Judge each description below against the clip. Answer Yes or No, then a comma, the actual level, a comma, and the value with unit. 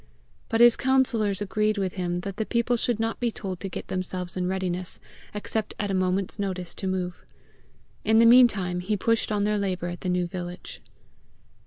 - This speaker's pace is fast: No, average, 190 wpm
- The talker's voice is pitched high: Yes, high, 195 Hz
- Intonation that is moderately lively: Yes, average, 3.3 semitones